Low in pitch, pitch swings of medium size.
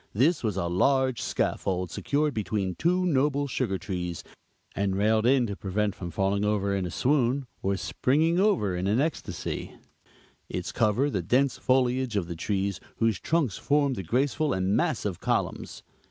No: low, 110 Hz; wide, 6.3 semitones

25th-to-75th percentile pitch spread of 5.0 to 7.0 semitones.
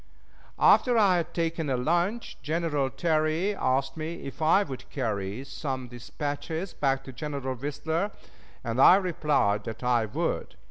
No: average, 4.4 semitones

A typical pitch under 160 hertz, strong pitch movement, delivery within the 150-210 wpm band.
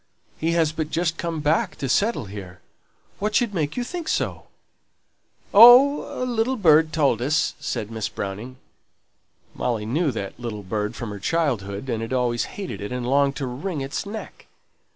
Yes: medium, 140 Hz; wide, 7.5 semitones; average, 175 wpm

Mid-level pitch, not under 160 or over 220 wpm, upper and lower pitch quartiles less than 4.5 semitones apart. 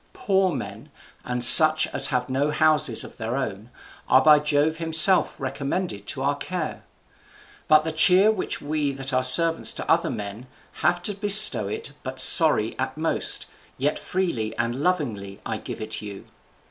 No: medium, 150 Hz; average, 165 wpm; average, 4.9 semitones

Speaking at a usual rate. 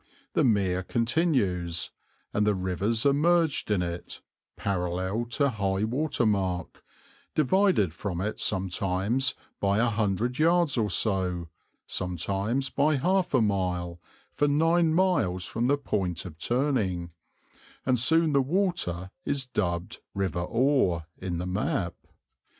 No: slow, 130 wpm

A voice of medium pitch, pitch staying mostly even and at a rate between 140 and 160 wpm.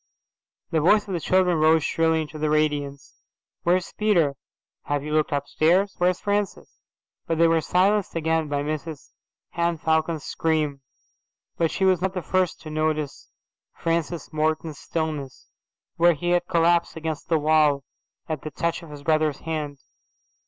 Yes: medium, 160 Hz; narrow, 2.1 semitones; average, 155 wpm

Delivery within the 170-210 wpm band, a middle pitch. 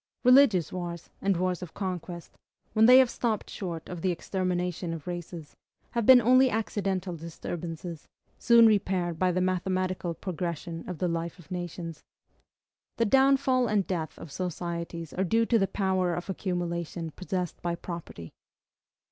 No: average, 150 wpm; medium, 180 Hz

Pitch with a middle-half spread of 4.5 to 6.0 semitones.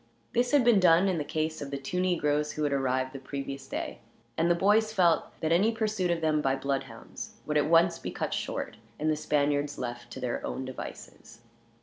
Yes: average, 4.8 semitones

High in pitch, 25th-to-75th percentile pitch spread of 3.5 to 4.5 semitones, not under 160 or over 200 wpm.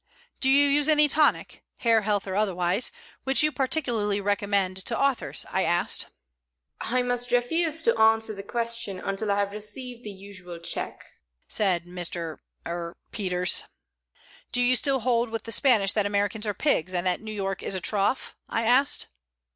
Yes: high, 215 Hz; average, 4.2 semitones; average, 170 wpm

